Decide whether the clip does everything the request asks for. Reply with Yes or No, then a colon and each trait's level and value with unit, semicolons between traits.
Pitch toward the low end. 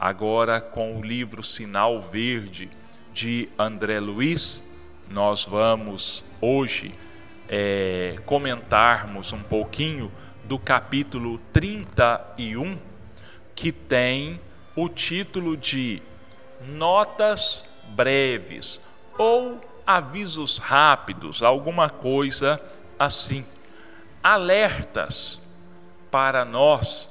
Yes: low, 115 Hz